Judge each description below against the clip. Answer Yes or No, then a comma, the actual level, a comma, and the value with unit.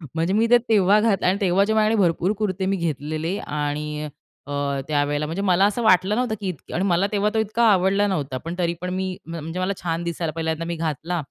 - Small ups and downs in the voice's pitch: No, average, 3.7 semitones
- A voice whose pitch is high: No, medium, 180 Hz